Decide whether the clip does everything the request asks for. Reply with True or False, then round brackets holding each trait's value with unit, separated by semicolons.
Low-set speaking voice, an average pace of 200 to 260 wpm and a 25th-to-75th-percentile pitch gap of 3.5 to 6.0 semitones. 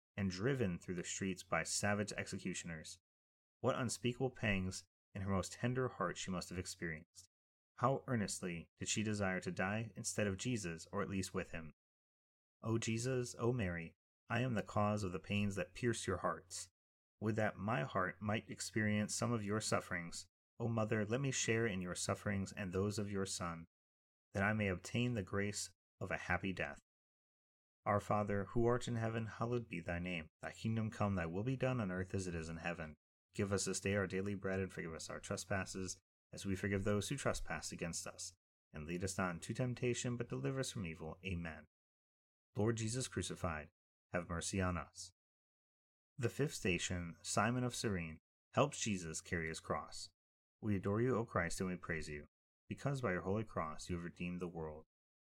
False (95 Hz; 190 wpm; 4.0 semitones)